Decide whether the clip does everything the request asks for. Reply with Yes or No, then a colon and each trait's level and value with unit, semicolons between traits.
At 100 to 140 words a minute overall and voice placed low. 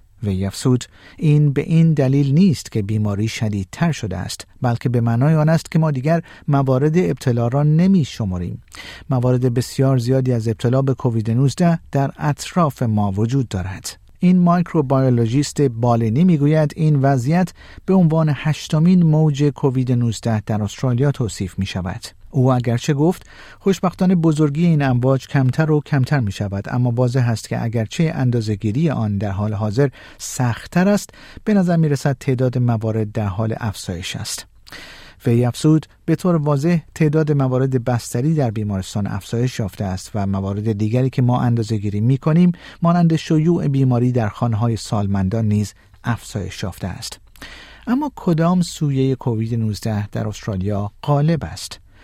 No: average, 150 wpm; low, 130 Hz